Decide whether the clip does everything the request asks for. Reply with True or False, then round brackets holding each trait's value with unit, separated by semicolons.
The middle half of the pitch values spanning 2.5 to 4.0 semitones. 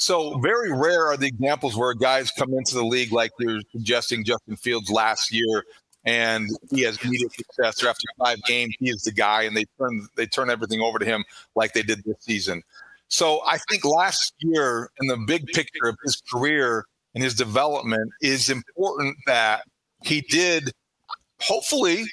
True (3.3 semitones)